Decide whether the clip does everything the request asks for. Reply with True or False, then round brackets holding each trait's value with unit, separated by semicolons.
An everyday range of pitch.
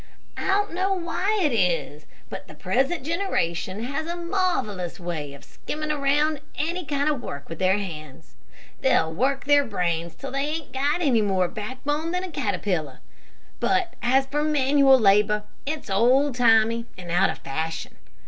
False (8.4 semitones)